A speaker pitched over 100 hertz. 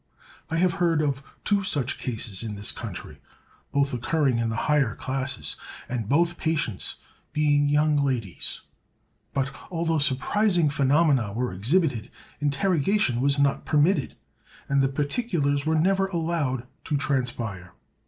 Yes: medium, 140 Hz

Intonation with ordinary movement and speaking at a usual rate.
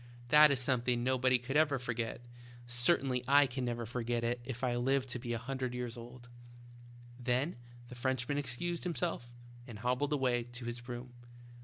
No: narrow, 1.8 semitones; average, 180 wpm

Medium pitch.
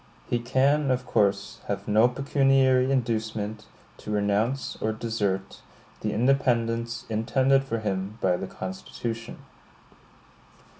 No: low, 115 Hz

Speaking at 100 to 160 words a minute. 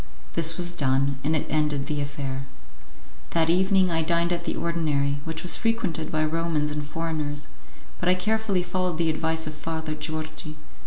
No: average, 170 wpm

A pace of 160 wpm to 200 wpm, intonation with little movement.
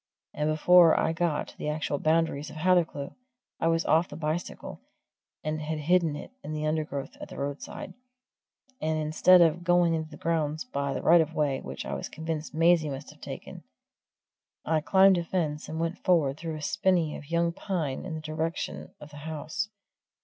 Yes: average, 190 wpm; narrow, 1.9 semitones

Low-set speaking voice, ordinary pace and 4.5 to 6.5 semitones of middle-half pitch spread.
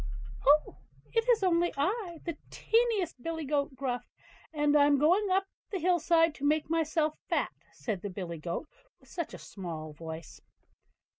No: very high, 305 Hz; average, 165 wpm; average, 5.2 semitones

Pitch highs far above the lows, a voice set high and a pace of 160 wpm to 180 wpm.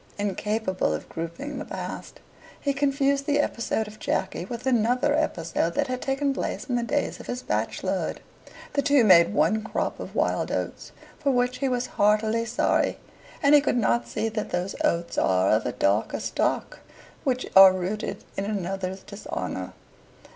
Yes: wide, 6.3 semitones; high, 220 Hz; average, 170 wpm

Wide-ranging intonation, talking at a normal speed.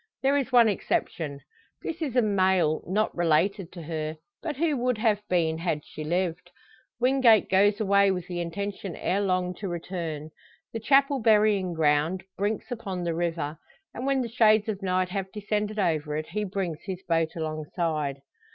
No: average, 4.6 semitones; average, 170 wpm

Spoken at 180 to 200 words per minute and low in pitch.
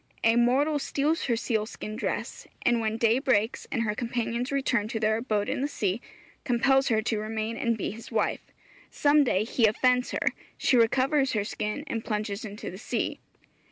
No: average, 185 wpm; high, 230 Hz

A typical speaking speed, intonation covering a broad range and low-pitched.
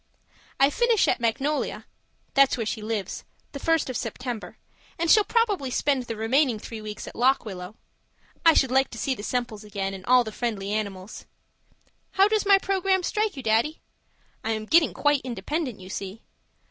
No: average, 180 wpm; wide, 6.1 semitones; very high, 250 Hz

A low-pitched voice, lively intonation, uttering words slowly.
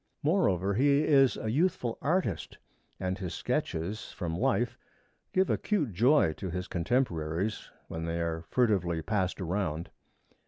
Yes: low, 100 Hz; wide, 7.2 semitones; slow, 130 wpm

